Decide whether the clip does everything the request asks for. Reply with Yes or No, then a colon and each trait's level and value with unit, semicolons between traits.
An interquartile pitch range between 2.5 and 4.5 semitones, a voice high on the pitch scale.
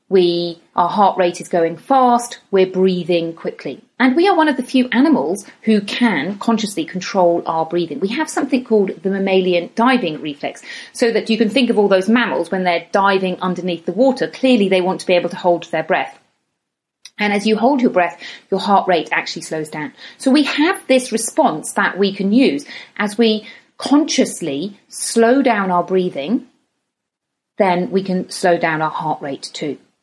No: wide, 5.4 semitones; high, 200 Hz